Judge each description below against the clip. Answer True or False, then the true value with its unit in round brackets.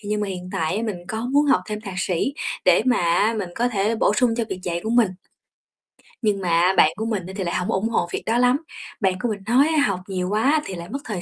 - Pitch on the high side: True (210 Hz)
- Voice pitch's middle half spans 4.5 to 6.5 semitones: False (4.1 semitones)